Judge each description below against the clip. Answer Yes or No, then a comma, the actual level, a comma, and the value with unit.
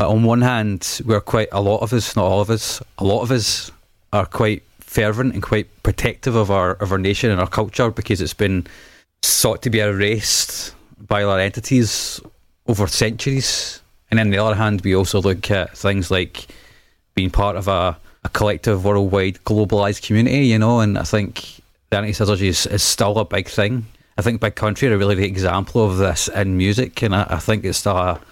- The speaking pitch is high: No, low, 105 Hz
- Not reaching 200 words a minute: No, fast, 205 wpm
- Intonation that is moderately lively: No, narrow, 2.3 semitones